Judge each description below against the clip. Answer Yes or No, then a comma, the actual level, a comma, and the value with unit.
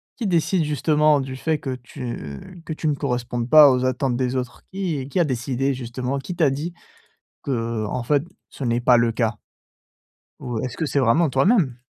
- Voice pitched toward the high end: No, low, 135 Hz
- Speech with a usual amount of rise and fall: Yes, average, 3.9 semitones